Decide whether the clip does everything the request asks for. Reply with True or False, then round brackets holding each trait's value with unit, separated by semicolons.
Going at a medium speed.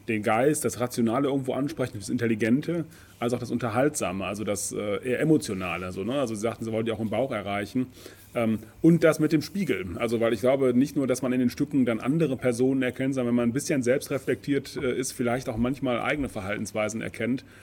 False (210 wpm)